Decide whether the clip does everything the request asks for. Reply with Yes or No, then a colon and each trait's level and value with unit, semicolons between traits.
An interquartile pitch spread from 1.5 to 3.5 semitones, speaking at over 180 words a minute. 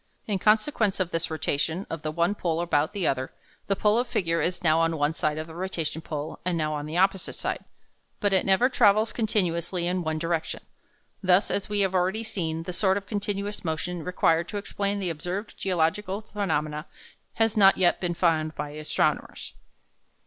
No: average, 3.9 semitones; average, 190 wpm